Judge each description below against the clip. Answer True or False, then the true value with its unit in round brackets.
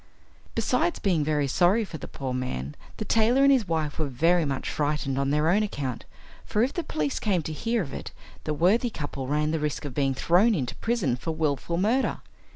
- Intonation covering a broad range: True (6.7 semitones)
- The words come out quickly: True (210 wpm)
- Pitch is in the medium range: True (155 Hz)